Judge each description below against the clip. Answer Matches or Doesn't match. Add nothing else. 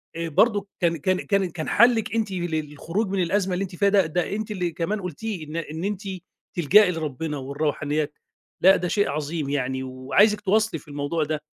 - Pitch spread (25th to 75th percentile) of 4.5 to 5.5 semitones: Matches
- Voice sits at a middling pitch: Matches